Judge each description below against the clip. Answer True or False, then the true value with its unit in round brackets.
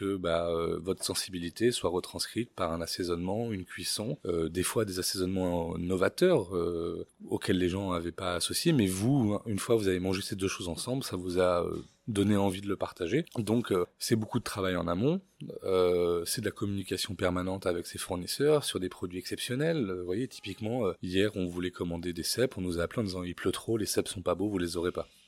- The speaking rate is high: True (225 wpm)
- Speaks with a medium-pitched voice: False (95 Hz)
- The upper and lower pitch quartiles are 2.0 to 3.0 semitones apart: False (3.4 semitones)